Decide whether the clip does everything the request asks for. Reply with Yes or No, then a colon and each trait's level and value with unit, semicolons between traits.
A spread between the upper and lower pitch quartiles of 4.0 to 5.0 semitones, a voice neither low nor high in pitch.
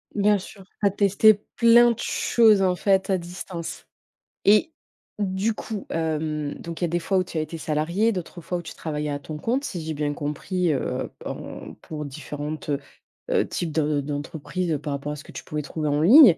Yes: average, 4.5 semitones; medium, 170 Hz